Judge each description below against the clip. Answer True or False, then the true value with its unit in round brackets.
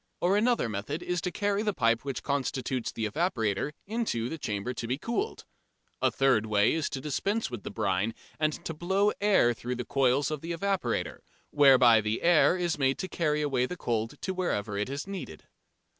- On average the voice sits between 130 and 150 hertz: True (140 Hz)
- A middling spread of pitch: False (7.4 semitones)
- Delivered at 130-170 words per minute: False (190 wpm)